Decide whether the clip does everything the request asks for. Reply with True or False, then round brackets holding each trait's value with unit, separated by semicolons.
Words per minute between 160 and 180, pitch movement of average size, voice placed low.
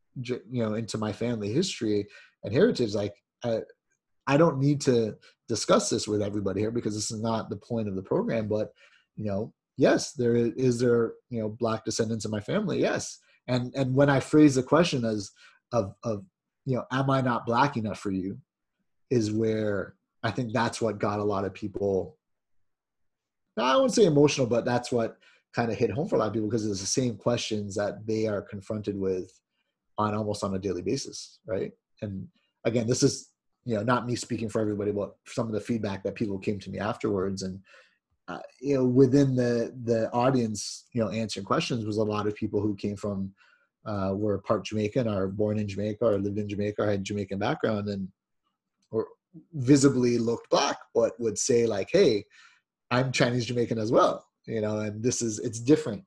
False (200 wpm; 3.0 semitones; 110 Hz)